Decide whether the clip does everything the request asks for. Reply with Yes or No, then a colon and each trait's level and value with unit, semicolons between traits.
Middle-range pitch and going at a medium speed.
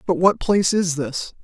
No: medium, 175 Hz; fast, 210 wpm